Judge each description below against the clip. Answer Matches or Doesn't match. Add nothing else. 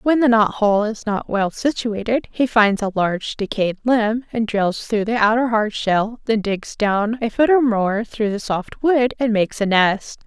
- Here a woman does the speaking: Matches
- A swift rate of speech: Matches